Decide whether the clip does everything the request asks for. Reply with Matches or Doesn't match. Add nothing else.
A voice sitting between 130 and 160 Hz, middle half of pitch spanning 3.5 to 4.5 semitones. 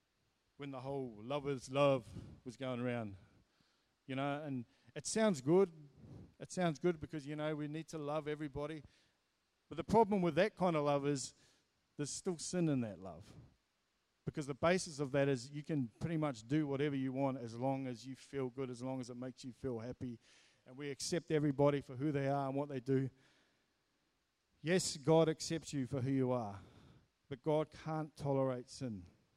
Doesn't match